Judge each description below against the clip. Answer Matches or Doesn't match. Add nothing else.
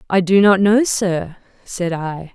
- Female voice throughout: Matches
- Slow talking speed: Doesn't match